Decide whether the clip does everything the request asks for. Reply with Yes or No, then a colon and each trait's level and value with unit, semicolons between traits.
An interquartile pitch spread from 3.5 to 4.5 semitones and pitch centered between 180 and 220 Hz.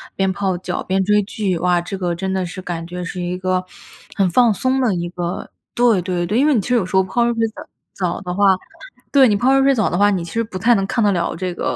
Yes: average, 3.9 semitones; high, 190 Hz